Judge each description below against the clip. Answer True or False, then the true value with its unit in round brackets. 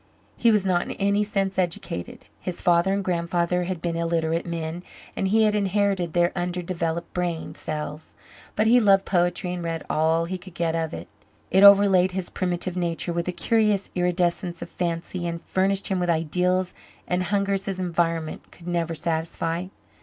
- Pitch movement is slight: True (2.2 semitones)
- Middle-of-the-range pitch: True (175 Hz)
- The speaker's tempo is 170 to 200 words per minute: True (175 wpm)